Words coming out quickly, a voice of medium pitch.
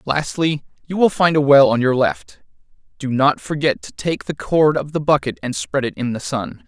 Yes: fast, 225 wpm; medium, 145 Hz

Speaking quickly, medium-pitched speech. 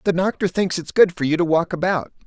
Yes: fast, 265 wpm; medium, 175 Hz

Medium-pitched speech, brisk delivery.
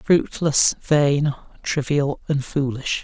No: medium, 145 Hz; slow, 100 wpm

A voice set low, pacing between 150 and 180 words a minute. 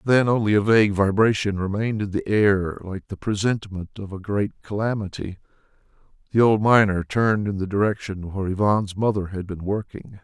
Yes: low, 100 Hz; average, 170 wpm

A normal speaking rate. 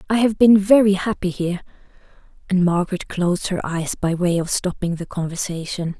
Yes: average, 170 wpm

